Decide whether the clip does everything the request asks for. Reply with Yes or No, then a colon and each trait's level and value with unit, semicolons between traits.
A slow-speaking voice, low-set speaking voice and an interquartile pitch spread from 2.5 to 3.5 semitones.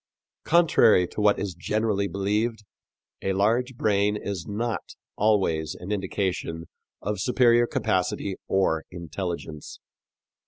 Yes: slow, 110 wpm; low, 100 Hz; average, 3.2 semitones